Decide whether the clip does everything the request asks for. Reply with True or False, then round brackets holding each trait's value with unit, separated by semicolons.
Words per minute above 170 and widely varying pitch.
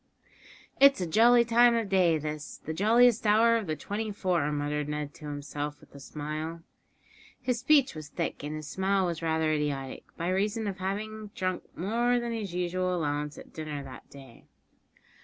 True (180 wpm; 6.4 semitones)